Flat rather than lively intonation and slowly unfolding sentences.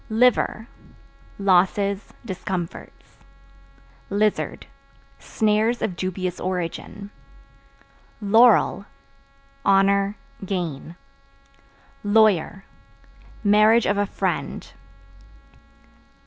Yes: narrow, 2.3 semitones; slow, 60 wpm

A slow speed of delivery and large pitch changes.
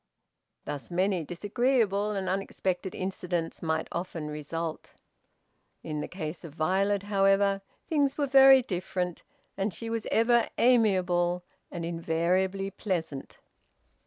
No: slow, 115 wpm; average, 3.3 semitones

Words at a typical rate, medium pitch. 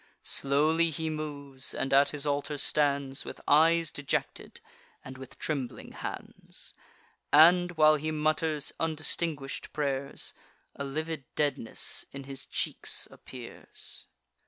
No: slow, 115 wpm; medium, 145 Hz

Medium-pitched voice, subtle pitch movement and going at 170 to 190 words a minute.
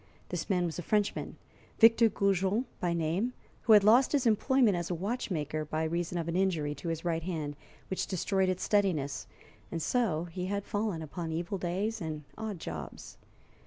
No: medium, 180 Hz; average, 4.2 semitones; average, 180 wpm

